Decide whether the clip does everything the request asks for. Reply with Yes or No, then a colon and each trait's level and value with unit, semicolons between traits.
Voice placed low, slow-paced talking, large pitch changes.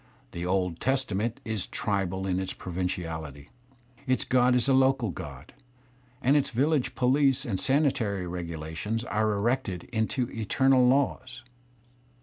Yes: low, 110 Hz; slow, 130 wpm; wide, 6.1 semitones